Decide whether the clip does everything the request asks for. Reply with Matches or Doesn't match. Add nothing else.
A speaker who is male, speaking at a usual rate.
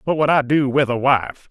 Doesn't match